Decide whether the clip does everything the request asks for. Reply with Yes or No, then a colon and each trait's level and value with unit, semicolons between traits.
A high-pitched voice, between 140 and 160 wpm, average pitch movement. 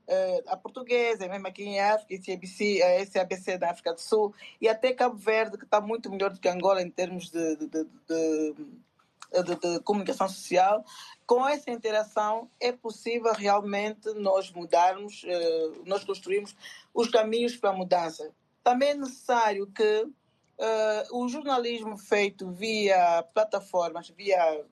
Yes: high, 200 Hz; average, 150 wpm; average, 3.6 semitones